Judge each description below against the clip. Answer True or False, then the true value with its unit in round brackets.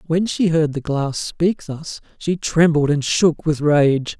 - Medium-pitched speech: True (155 Hz)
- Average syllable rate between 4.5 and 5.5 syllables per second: False (3.6 syllables/s)